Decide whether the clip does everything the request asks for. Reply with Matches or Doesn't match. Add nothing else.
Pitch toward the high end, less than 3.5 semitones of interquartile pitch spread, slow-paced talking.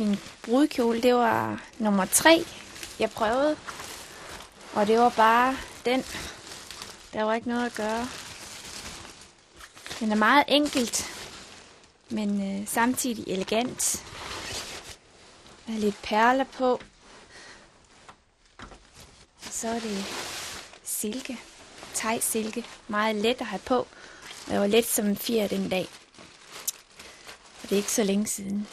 Matches